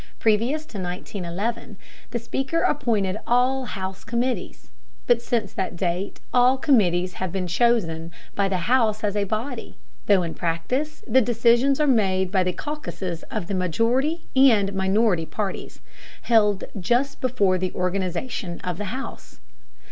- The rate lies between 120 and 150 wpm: Yes, average, 145 wpm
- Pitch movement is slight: No, average, 4.9 semitones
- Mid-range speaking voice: No, high, 210 Hz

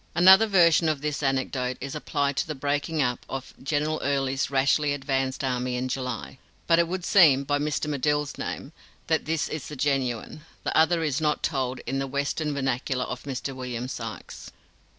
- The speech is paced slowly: No, average, 180 wpm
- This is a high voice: No, medium, 140 Hz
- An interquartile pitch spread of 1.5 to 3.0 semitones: Yes, narrow, 2.5 semitones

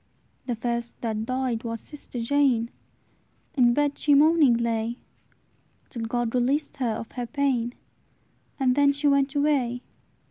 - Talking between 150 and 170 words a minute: No, average, 140 wpm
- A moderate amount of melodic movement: Yes, average, 3.2 semitones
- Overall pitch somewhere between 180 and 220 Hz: No, very high, 250 Hz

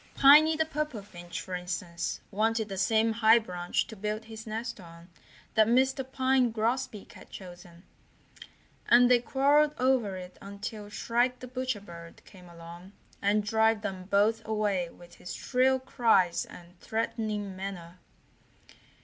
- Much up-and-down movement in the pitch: No, average, 4.8 semitones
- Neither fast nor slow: Yes, average, 145 wpm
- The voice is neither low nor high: No, high, 215 Hz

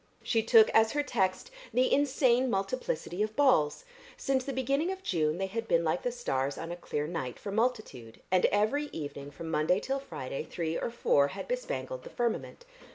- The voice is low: No, high, 215 Hz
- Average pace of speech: Yes, average, 190 wpm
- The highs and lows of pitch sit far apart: Yes, wide, 8.0 semitones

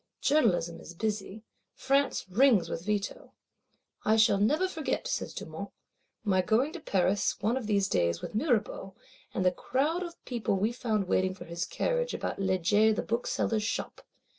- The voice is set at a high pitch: Yes, high, 215 Hz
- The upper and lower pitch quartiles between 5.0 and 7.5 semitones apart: Yes, average, 5.3 semitones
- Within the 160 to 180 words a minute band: Yes, average, 165 wpm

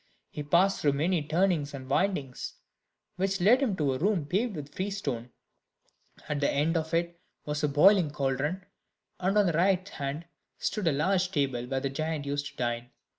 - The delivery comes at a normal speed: Yes, average, 180 wpm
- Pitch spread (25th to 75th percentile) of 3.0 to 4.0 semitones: No, average, 4.9 semitones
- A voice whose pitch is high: No, medium, 155 Hz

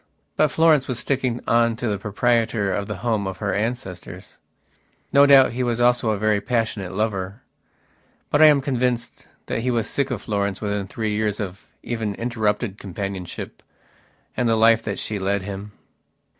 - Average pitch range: Yes, average, 3.2 semitones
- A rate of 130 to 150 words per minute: No, average, 170 wpm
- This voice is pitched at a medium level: No, low, 110 Hz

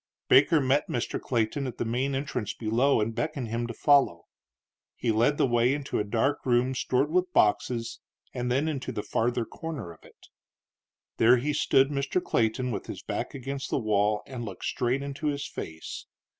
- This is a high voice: No, low, 125 Hz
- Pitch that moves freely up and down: No, average, 3.5 semitones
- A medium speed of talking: Yes, average, 185 wpm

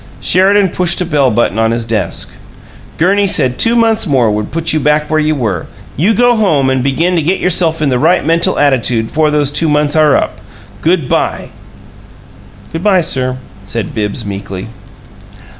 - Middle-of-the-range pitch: Yes, medium, 150 Hz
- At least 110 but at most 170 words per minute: No, average, 180 wpm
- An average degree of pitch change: No, wide, 6.0 semitones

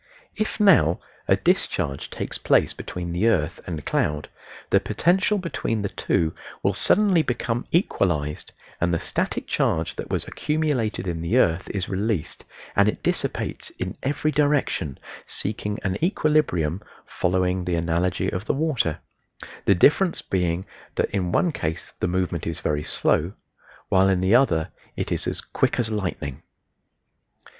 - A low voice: Yes, very low, 95 Hz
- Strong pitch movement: Yes, wide, 7.4 semitones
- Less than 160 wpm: Yes, average, 150 wpm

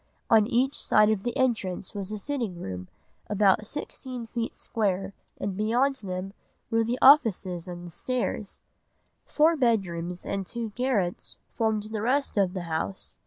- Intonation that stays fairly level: No, average, 4.4 semitones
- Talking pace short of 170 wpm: Yes, average, 155 wpm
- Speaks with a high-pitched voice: Yes, high, 215 Hz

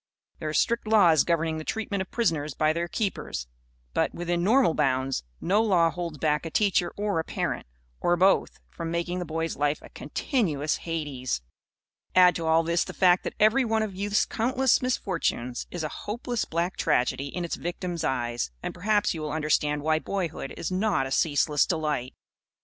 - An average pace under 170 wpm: No, average, 185 wpm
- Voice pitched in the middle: Yes, medium, 170 Hz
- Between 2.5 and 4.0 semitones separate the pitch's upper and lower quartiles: No, average, 4.5 semitones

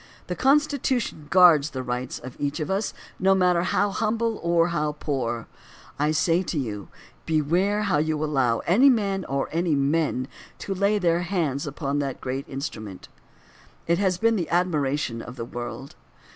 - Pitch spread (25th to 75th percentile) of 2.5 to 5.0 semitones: No, wide, 5.5 semitones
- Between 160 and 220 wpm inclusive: Yes, average, 170 wpm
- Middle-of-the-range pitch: Yes, medium, 160 Hz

